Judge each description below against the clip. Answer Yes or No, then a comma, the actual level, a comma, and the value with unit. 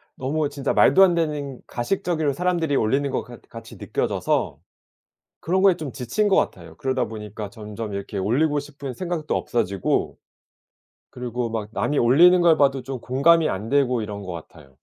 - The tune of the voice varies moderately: No, wide, 5.7 semitones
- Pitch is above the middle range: No, low, 135 Hz